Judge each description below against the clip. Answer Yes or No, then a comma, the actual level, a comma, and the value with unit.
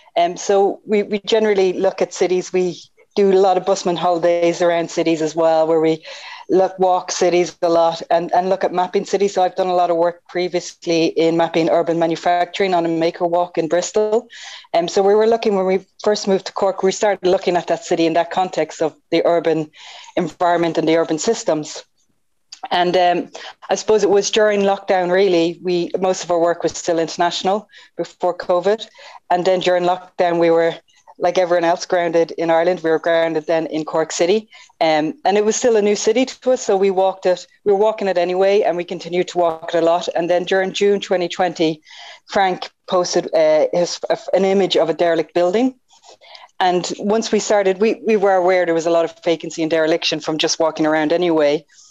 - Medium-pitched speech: Yes, medium, 180 Hz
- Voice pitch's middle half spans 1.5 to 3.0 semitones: Yes, average, 2.7 semitones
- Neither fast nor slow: No, fast, 210 wpm